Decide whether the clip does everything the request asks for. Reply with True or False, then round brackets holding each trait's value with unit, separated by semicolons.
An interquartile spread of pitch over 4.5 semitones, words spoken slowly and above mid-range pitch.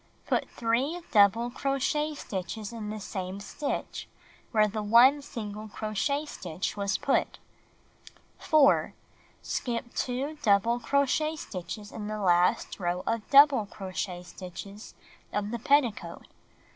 True (5.3 semitones; 130 wpm; 215 Hz)